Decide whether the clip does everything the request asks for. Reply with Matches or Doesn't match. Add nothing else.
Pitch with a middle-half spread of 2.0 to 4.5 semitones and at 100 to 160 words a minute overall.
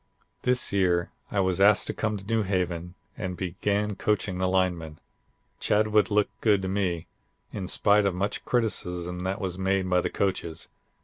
Doesn't match